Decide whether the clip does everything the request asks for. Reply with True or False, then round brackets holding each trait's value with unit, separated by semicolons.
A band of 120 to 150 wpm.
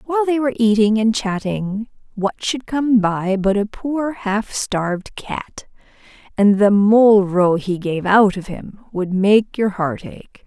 False (170 wpm)